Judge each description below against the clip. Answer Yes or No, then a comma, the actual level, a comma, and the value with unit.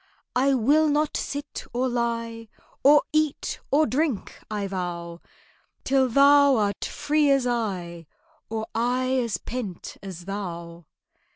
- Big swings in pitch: Yes, wide, 5.9 semitones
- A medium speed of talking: No, slow, 125 wpm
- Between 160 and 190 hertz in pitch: No, high, 240 Hz